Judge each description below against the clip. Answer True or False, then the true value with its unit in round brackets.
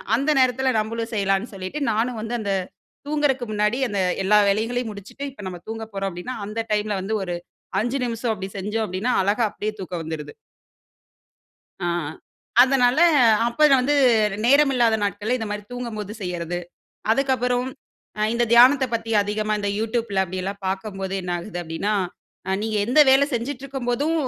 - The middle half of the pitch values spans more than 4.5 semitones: False (3.9 semitones)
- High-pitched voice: True (220 Hz)